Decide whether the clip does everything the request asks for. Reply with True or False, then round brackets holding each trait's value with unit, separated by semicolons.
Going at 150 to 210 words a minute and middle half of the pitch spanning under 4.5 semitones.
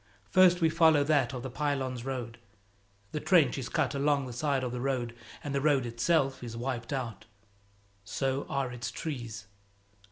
True (170 wpm; 3.1 semitones)